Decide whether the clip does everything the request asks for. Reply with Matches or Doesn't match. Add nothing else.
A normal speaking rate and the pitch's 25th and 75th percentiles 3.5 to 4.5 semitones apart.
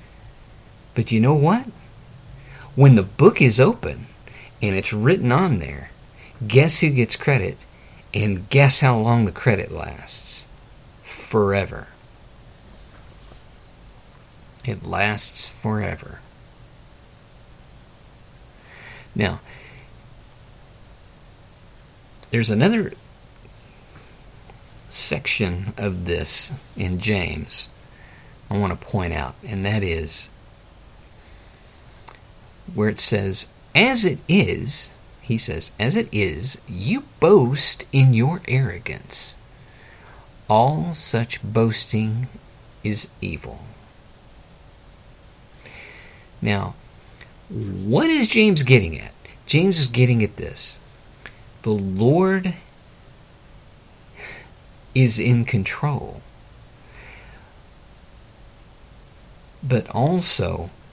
Doesn't match